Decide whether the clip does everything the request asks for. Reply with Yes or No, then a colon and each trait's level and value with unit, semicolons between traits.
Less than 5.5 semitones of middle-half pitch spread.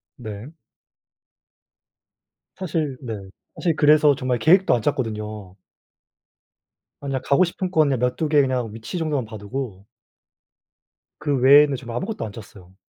Yes: average, 5.1 semitones